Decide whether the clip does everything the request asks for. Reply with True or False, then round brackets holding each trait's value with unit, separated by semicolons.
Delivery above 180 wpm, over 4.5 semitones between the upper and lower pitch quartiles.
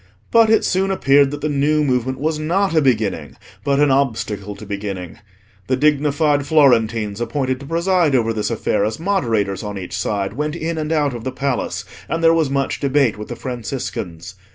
True (190 wpm; 5.4 semitones)